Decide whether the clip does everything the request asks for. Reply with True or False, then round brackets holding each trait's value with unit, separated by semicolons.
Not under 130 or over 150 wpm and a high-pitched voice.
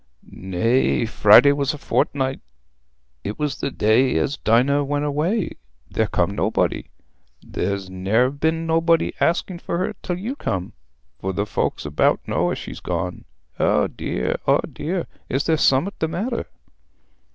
False (140 wpm; 135 Hz)